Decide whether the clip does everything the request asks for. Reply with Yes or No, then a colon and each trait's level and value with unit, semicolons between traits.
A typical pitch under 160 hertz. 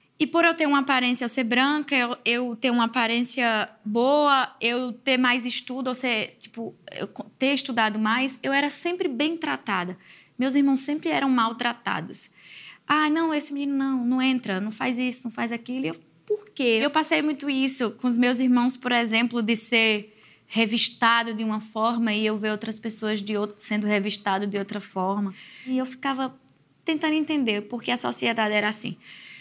No: high, 245 Hz